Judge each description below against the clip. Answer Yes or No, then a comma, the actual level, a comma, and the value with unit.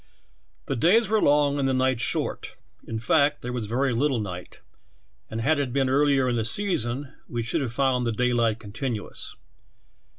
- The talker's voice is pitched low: Yes, low, 130 Hz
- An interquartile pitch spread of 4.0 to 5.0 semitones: No, average, 3.5 semitones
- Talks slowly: No, average, 175 wpm